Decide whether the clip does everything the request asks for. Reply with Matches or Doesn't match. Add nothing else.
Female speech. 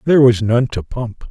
Doesn't match